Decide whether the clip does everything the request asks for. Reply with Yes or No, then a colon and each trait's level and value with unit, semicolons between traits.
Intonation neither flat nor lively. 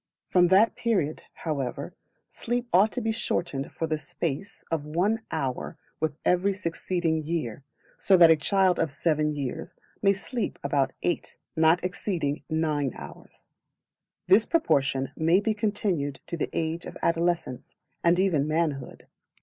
Yes: average, 4.4 semitones